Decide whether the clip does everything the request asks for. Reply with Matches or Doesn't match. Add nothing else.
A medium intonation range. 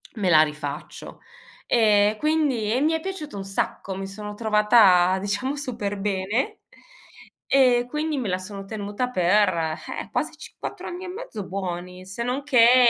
Matches